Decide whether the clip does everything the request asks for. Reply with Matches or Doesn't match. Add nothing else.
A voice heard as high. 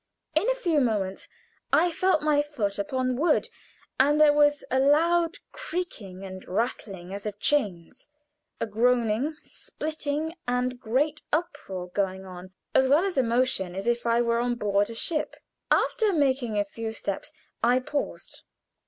Matches